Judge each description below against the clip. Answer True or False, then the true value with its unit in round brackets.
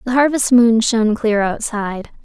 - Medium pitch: False (225 Hz)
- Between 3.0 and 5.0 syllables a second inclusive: True (4.9 syllables/s)